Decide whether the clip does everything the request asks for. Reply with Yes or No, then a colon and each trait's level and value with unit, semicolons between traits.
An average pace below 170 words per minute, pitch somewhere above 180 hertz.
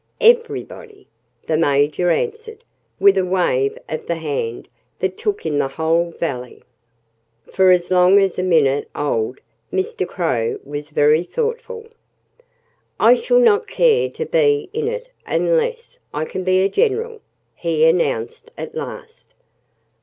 Yes: average, 140 wpm; high, 190 Hz